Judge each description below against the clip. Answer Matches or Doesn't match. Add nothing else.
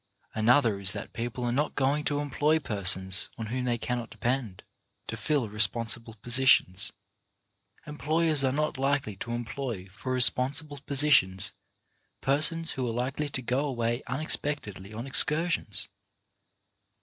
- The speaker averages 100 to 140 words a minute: Matches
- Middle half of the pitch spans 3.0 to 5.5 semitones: Matches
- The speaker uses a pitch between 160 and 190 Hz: Doesn't match